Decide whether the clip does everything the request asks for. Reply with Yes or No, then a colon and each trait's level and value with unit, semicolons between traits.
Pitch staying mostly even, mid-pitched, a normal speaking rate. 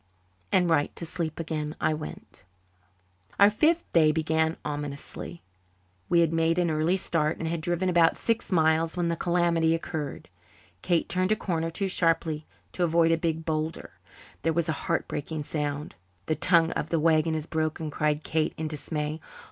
Yes: narrow, 1.5 semitones; medium, 160 Hz; average, 170 wpm